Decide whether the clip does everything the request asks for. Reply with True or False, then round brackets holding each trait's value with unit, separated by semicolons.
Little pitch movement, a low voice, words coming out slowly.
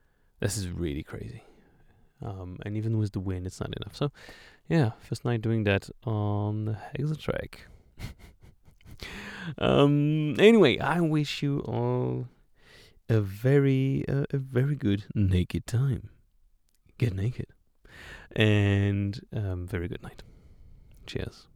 False (5.6 semitones; 110 Hz; 125 wpm)